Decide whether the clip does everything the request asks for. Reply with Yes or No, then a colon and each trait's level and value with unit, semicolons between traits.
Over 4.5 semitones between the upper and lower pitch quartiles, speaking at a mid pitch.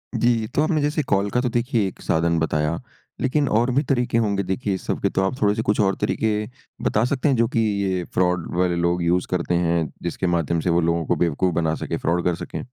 No: average, 5.3 semitones; very low, 95 Hz